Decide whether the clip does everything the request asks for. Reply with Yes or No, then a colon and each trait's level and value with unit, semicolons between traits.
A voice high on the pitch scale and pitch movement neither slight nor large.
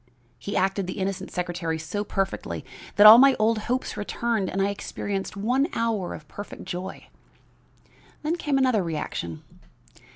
Yes: high, 200 Hz; average, 3.7 semitones